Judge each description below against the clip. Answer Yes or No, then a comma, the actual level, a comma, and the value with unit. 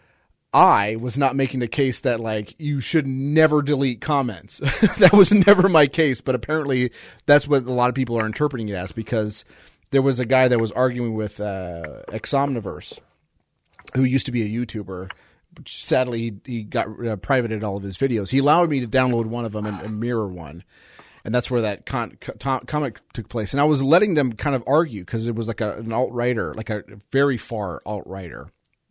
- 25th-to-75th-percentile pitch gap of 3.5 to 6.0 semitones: Yes, average, 4.1 semitones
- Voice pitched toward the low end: Yes, low, 125 Hz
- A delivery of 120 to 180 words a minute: No, fast, 205 wpm